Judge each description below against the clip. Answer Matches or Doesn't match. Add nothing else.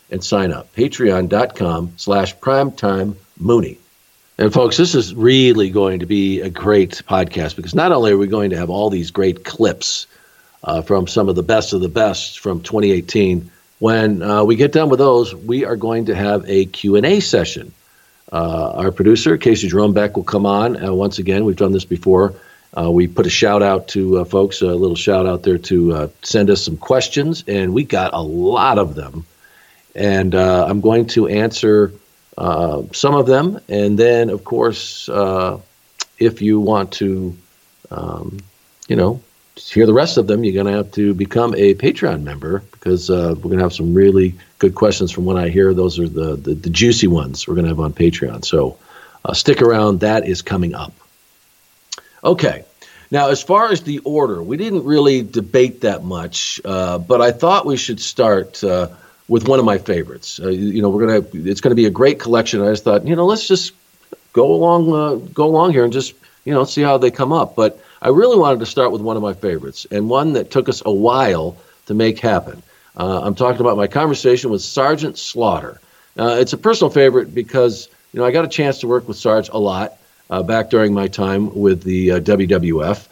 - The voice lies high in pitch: Doesn't match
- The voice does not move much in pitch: Doesn't match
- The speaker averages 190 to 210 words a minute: Matches